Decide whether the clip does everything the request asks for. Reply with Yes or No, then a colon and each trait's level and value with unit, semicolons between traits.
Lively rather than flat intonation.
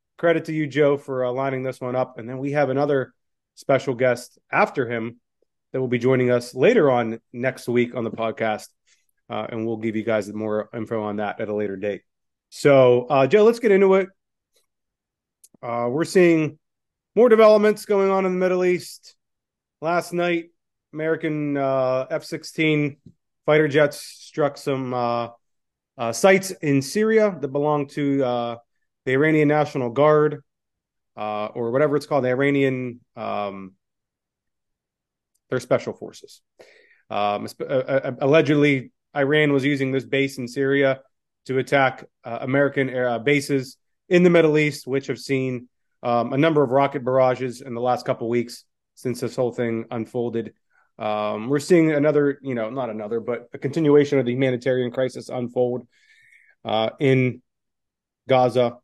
No: average, 3.7 semitones